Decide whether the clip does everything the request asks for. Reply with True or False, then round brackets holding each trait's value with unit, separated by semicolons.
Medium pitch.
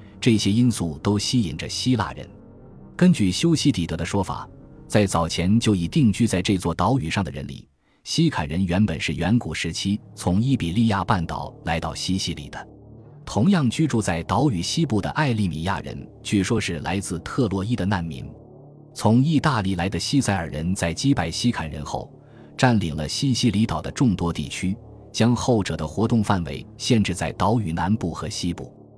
False (100 Hz)